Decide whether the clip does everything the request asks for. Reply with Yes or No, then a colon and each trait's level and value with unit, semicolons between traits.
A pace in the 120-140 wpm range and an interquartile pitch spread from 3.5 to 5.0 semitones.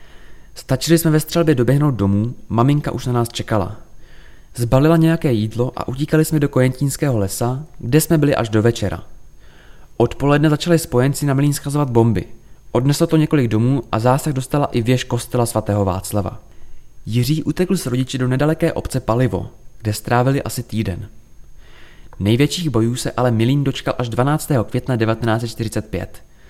No: average, 150 wpm; average, 4.4 semitones